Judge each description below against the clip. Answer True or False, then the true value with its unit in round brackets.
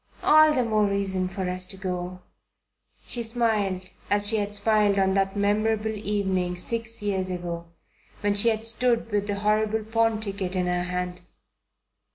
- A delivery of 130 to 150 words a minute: False (165 wpm)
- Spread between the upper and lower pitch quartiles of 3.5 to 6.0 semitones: False (2.8 semitones)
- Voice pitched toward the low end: False (205 Hz)